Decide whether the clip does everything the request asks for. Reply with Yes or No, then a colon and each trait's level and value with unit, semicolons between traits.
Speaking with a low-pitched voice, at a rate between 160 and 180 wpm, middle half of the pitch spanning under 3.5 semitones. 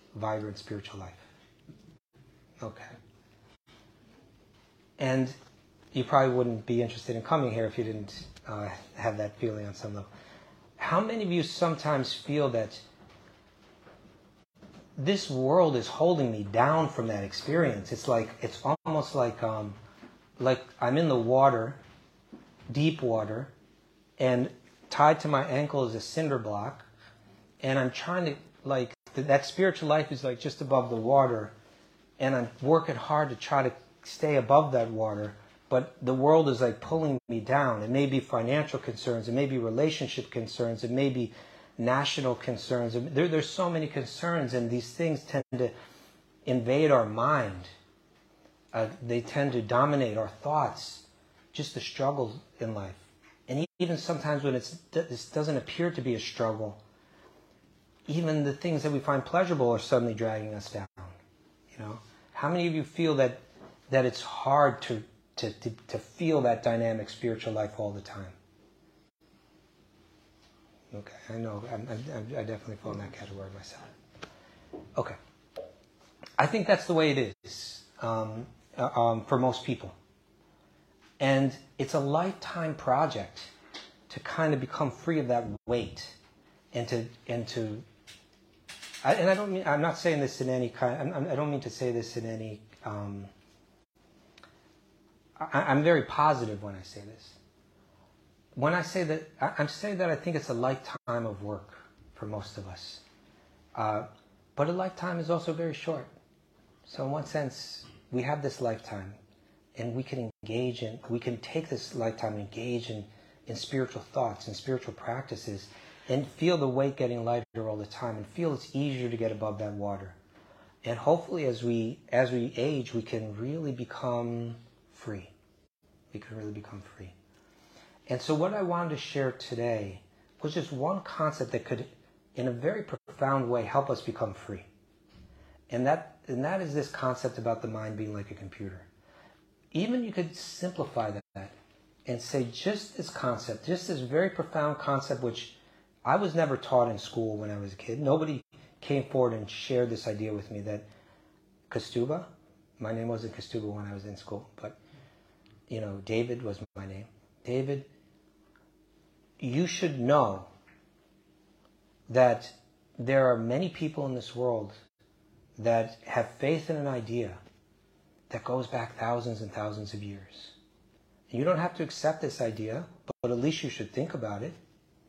No: low, 120 Hz; average, 165 wpm; average, 4.8 semitones